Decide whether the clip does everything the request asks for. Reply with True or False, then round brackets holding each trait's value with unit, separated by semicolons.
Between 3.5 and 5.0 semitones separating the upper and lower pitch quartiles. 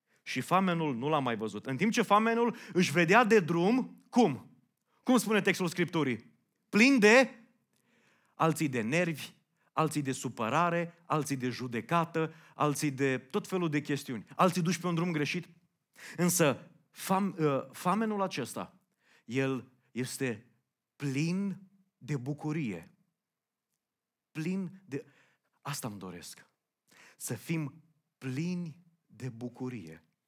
False (5.4 semitones)